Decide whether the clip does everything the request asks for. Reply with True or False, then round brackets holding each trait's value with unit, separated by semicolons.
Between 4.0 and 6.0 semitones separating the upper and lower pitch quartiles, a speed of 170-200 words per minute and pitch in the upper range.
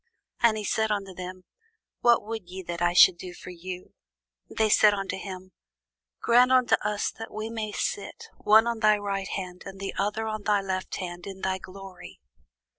False (2.6 semitones; 190 wpm; 195 Hz)